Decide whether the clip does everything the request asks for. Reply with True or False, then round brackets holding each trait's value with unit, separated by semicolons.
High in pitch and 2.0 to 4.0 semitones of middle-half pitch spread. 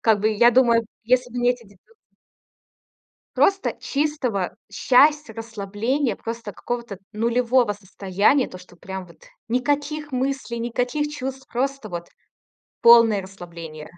False (235 Hz; 4.4 semitones)